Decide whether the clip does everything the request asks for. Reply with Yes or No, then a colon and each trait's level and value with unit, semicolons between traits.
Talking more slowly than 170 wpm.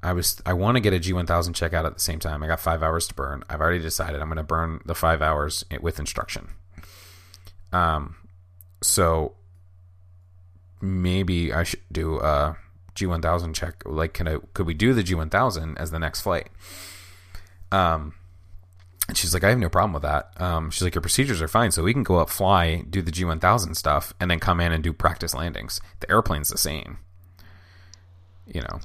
No: average, 195 wpm